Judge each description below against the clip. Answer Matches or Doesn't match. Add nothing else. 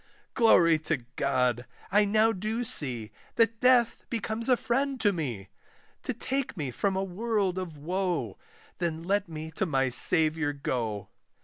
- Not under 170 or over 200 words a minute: Doesn't match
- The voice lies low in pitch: Doesn't match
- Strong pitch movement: Matches